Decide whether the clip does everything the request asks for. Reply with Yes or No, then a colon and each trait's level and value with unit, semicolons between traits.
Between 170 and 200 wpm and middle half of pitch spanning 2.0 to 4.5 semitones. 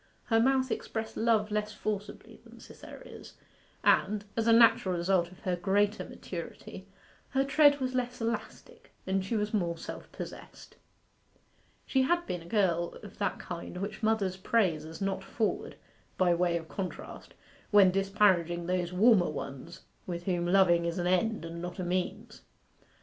No: average, 160 wpm; average, 4.1 semitones